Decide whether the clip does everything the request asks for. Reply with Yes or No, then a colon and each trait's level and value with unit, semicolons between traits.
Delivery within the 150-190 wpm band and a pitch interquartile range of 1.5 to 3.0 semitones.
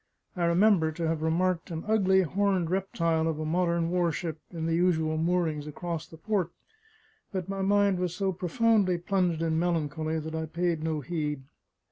Yes: average, 170 wpm; narrow, 2.5 semitones